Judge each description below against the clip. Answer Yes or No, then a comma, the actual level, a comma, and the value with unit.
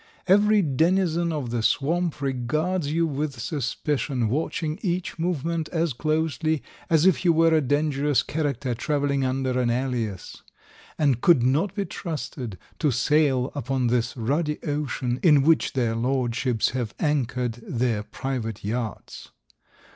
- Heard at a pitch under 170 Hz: Yes, medium, 140 Hz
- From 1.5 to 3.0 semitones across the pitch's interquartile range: No, average, 4.4 semitones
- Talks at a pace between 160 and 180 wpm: No, slow, 135 wpm